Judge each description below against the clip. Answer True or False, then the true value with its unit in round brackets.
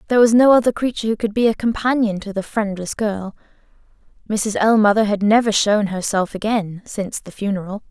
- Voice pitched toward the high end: True (210 Hz)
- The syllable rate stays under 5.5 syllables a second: False (5.9 syllables/s)